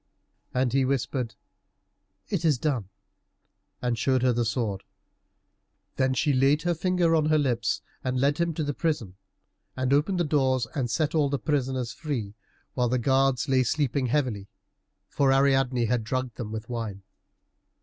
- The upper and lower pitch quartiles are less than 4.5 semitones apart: Yes, average, 3.3 semitones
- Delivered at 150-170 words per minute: Yes, average, 160 wpm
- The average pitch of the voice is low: Yes, low, 130 Hz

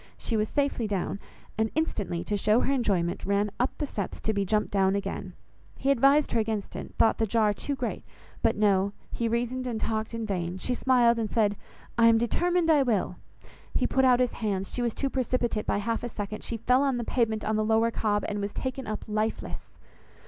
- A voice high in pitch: Yes, high, 225 Hz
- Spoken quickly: Yes, fast, 215 wpm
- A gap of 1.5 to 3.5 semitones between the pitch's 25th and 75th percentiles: Yes, average, 3.2 semitones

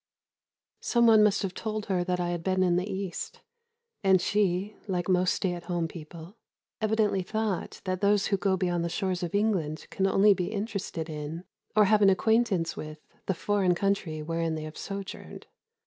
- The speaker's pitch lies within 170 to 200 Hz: Yes, medium, 185 Hz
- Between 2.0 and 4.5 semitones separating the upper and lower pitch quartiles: Yes, average, 2.8 semitones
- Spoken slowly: No, average, 185 wpm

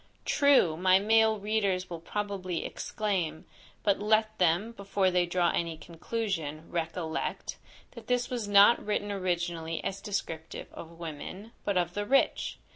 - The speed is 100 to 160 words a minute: Yes, average, 140 wpm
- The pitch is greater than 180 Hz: Yes, high, 190 Hz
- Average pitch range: Yes, average, 3.8 semitones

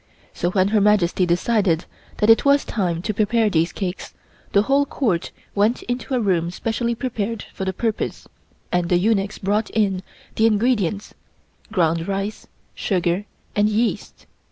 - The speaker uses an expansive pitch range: No, average, 3.6 semitones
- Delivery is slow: No, average, 155 wpm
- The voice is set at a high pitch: Yes, high, 205 Hz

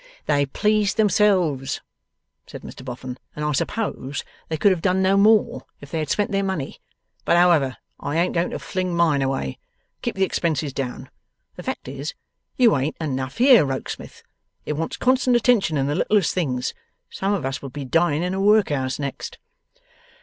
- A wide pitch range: Yes, wide, 6.2 semitones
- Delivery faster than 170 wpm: Yes, average, 180 wpm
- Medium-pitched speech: Yes, medium, 165 Hz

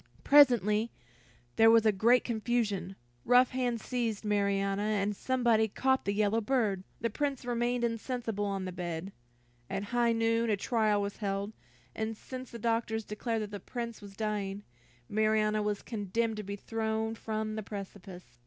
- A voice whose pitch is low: No, high, 220 Hz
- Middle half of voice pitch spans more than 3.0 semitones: No, narrow, 2.4 semitones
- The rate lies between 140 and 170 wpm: Yes, average, 160 wpm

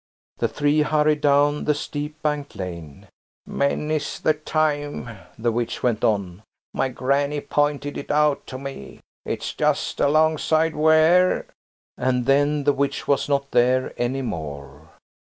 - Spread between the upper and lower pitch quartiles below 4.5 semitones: Yes, average, 3.6 semitones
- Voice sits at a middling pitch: Yes, medium, 145 Hz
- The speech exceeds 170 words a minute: No, slow, 135 wpm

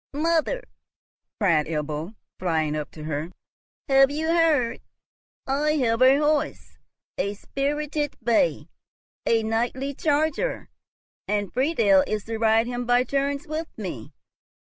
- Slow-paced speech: Yes, slow, 125 wpm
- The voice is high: Yes, high, 245 Hz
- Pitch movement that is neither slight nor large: No, wide, 6.5 semitones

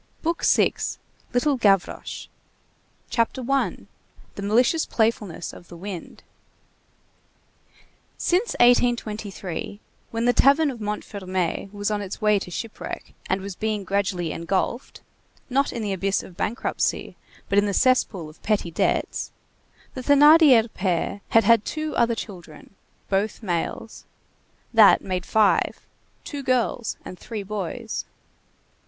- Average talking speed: No, slow, 125 wpm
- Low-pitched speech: No, high, 210 Hz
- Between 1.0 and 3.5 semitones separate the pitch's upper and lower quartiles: No, average, 4.0 semitones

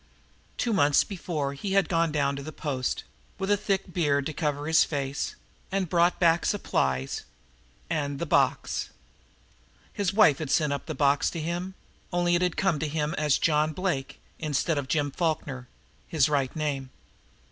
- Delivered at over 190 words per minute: No, average, 175 wpm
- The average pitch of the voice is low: No, medium, 155 Hz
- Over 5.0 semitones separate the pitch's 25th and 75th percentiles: No, average, 3.6 semitones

